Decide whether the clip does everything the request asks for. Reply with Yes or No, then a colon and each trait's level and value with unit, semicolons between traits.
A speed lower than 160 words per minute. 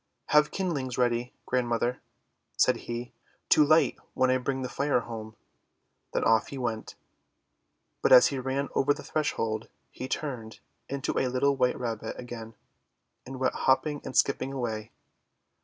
Yes: average, 150 wpm